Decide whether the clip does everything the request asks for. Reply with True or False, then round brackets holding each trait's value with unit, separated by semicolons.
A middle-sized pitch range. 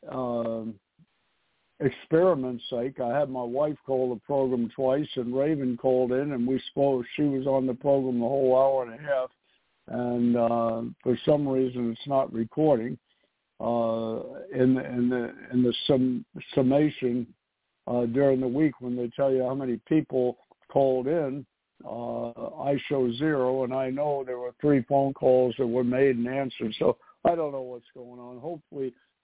False (2.2 semitones)